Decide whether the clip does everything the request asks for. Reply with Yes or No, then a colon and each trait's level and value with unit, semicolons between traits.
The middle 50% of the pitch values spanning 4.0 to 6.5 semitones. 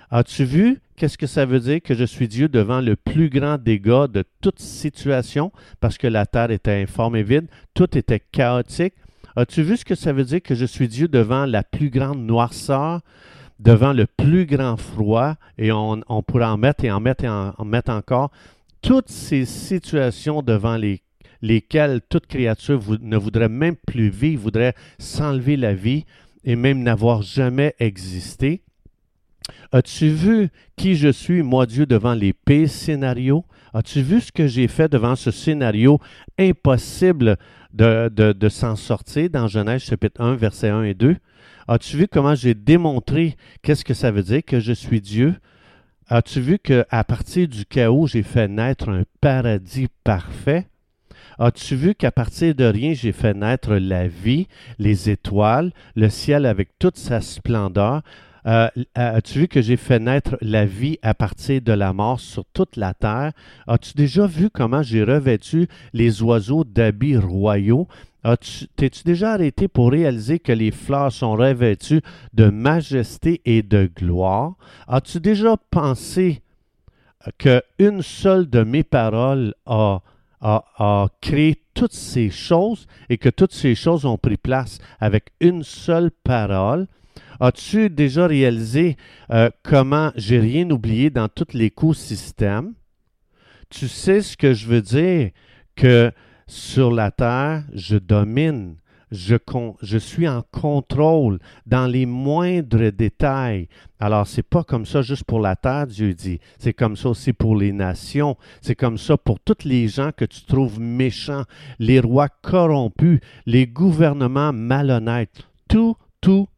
Yes: average, 5.0 semitones